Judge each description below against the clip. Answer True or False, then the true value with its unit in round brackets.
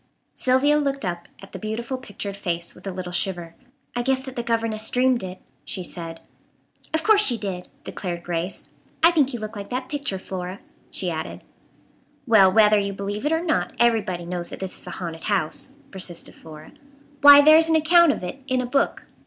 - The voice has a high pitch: True (215 Hz)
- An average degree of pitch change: False (6.5 semitones)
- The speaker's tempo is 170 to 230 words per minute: True (200 wpm)